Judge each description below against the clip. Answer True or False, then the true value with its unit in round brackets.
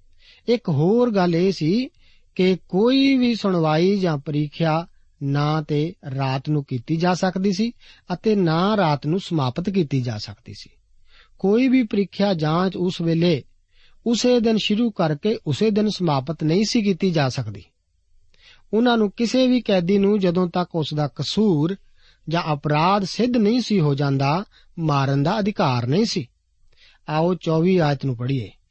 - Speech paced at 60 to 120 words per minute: False (155 wpm)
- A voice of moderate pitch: True (170 Hz)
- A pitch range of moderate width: False (6.0 semitones)